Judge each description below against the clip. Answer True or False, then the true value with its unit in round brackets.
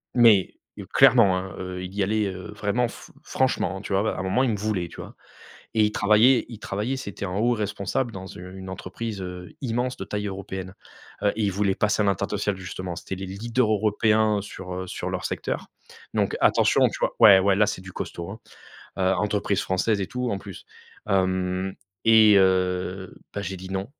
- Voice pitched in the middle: False (100 Hz)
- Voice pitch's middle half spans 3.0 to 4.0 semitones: False (2.4 semitones)